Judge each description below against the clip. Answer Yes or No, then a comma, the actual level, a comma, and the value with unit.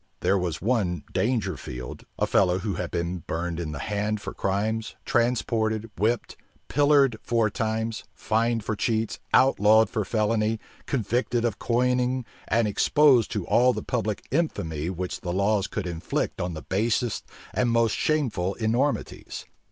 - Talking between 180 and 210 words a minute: No, average, 145 wpm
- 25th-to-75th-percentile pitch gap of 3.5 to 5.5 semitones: Yes, average, 3.8 semitones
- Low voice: Yes, low, 110 Hz